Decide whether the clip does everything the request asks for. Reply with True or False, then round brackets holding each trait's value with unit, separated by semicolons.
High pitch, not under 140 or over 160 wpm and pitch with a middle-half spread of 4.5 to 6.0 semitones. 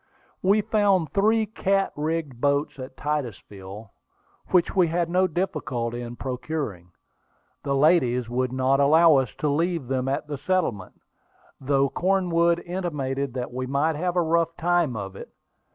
False (150 Hz; 150 wpm; 5.3 semitones)